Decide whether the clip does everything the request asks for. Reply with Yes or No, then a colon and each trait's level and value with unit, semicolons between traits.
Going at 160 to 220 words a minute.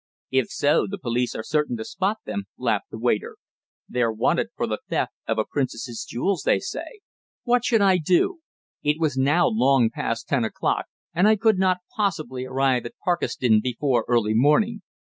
Yes: average, 180 wpm